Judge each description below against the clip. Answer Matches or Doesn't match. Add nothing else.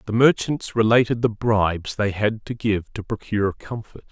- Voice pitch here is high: Doesn't match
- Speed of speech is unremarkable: Matches